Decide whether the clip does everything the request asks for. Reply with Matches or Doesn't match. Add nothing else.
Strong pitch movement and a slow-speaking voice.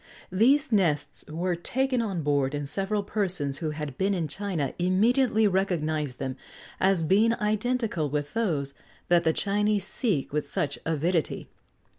Doesn't match